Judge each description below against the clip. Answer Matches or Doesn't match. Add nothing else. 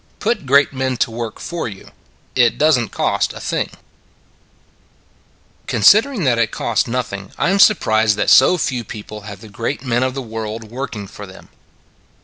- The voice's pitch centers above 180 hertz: Doesn't match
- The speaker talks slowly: Doesn't match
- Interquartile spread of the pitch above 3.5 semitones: Matches